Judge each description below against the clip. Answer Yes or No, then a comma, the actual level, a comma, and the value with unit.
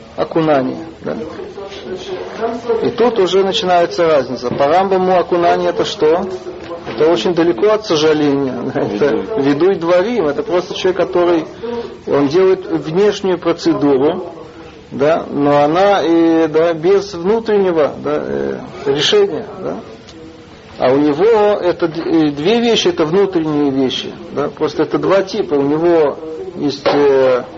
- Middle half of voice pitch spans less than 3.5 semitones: No, average, 4.8 semitones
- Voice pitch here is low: No, medium, 170 Hz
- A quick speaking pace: No, average, 125 wpm